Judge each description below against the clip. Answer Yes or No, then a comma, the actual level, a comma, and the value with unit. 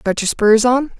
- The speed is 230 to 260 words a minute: Yes, fast, 240 wpm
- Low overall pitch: No, high, 235 Hz